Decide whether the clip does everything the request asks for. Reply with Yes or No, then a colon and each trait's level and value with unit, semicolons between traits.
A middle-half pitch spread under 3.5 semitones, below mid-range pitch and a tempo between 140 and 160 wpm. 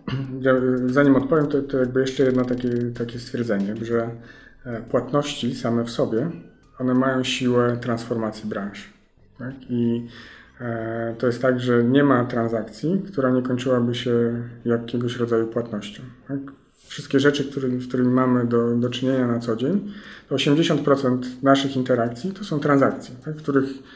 Yes: narrow, 2.4 semitones; low, 125 Hz; average, 150 wpm